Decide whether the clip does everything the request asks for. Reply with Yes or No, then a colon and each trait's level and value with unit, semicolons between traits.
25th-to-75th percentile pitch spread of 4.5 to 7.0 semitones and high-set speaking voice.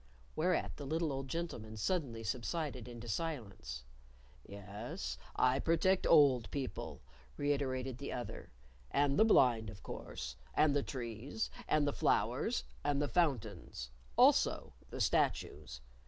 No: average, 5.1 semitones; low, 135 Hz